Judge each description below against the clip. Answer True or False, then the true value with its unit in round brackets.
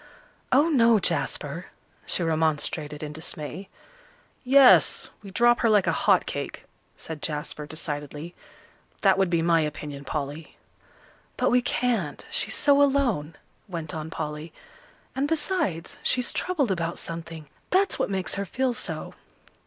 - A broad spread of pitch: True (8.0 semitones)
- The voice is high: False (170 Hz)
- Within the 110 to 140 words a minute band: True (135 wpm)